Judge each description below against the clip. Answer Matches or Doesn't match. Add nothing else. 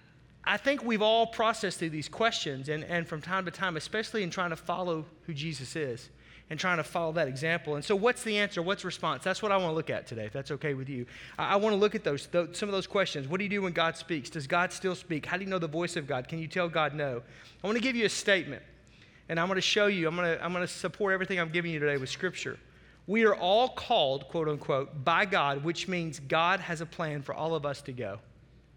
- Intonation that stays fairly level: Doesn't match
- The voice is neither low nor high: Matches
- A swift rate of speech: Matches